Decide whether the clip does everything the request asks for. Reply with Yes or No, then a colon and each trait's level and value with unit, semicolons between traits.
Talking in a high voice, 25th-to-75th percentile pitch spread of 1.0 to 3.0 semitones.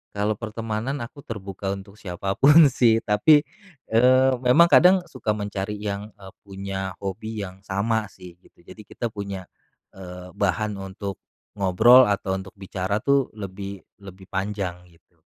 No: low, 100 Hz; average, 2.7 semitones